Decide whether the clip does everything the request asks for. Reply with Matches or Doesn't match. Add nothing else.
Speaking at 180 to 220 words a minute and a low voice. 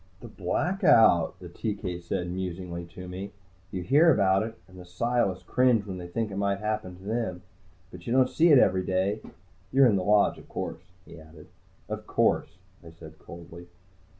Matches